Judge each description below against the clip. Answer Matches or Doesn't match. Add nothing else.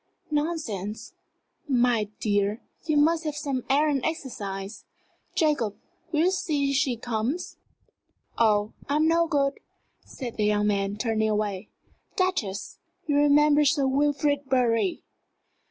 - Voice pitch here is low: Doesn't match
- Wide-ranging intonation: Matches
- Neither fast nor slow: Doesn't match